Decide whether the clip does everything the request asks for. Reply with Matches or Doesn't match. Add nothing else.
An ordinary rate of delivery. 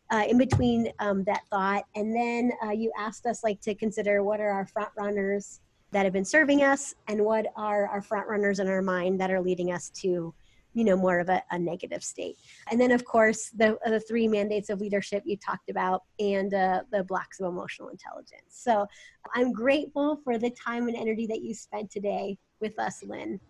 Doesn't match